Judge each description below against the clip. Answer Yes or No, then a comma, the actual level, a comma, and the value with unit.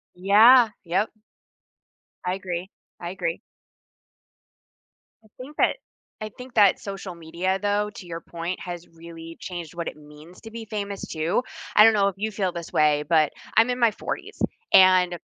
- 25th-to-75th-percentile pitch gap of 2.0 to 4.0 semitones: Yes, average, 3.7 semitones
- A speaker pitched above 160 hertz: Yes, medium, 185 Hz